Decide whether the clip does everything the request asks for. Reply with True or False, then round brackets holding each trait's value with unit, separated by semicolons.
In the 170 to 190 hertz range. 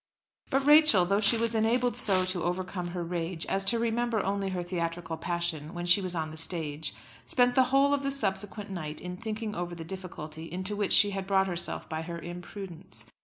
True (185 Hz)